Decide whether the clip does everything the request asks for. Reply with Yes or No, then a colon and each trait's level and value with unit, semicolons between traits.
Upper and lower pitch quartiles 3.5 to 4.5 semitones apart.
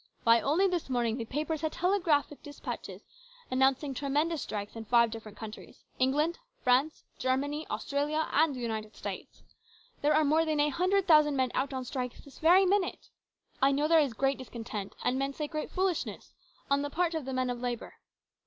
Yes: average, 3.8 semitones